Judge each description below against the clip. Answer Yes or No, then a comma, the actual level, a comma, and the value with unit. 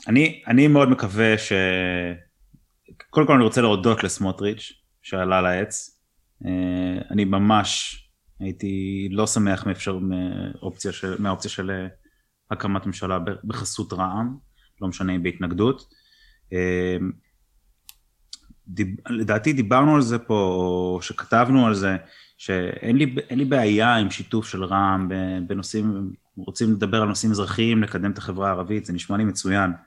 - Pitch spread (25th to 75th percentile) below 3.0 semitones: Yes, narrow, 2.6 semitones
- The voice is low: Yes, low, 100 Hz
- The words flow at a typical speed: Yes, average, 125 wpm